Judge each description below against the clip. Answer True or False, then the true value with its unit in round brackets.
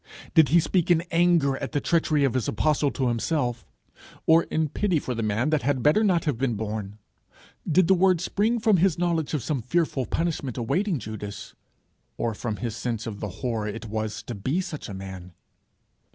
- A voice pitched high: False (140 Hz)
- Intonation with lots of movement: True (6.8 semitones)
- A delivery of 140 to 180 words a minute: False (195 wpm)